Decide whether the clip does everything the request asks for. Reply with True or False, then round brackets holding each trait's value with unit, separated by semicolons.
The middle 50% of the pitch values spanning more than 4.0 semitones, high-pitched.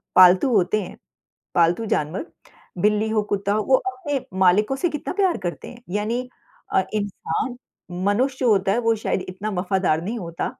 True (4.6 semitones; 210 Hz)